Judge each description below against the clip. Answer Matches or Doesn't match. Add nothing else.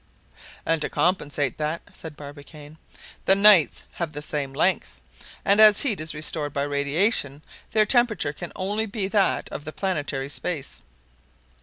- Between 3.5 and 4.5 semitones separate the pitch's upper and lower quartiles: Doesn't match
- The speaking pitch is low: Doesn't match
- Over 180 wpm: Doesn't match